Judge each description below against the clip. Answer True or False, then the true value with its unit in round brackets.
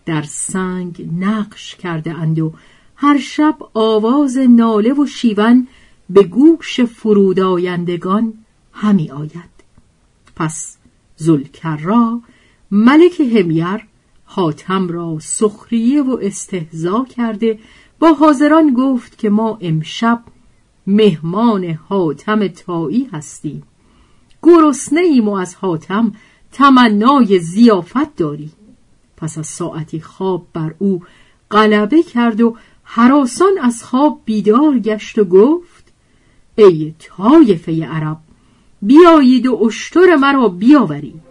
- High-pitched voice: True (215 Hz)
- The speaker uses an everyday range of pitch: False (6.4 semitones)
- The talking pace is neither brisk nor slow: False (100 wpm)